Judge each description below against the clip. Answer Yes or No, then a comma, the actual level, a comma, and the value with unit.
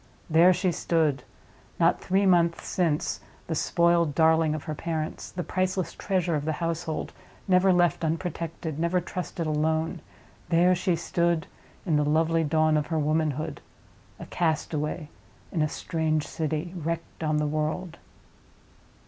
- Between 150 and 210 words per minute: No, slow, 135 wpm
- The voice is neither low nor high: Yes, medium, 165 Hz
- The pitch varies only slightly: Yes, narrow, 1.9 semitones